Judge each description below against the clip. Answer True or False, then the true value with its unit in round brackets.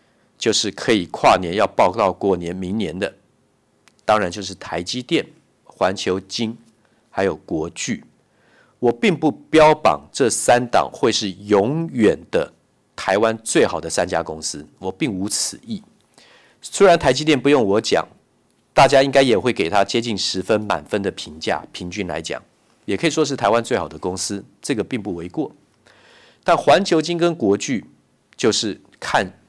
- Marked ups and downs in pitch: True (7.9 semitones)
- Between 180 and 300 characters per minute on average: True (230 characters per minute)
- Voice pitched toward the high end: False (115 Hz)